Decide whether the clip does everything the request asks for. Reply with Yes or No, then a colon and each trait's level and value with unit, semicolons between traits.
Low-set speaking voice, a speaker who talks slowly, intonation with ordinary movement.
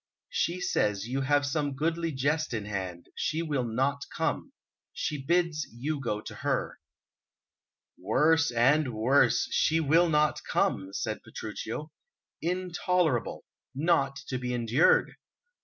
No: medium, 145 Hz; slow, 125 wpm; average, 4.7 semitones